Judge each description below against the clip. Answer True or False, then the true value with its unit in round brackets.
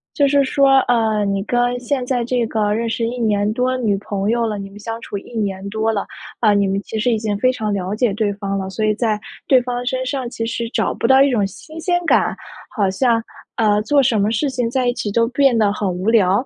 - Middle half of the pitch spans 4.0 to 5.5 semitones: False (3.3 semitones)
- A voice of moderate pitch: False (225 Hz)